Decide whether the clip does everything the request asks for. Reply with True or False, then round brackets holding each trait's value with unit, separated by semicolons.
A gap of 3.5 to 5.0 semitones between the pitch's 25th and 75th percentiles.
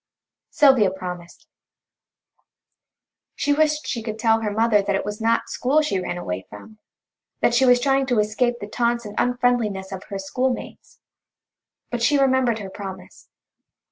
True (3.8 semitones)